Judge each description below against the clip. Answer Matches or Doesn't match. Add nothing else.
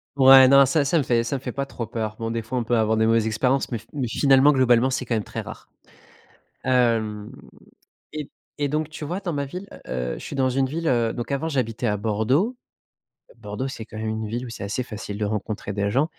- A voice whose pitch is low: Matches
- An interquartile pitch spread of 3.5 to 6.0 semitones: Matches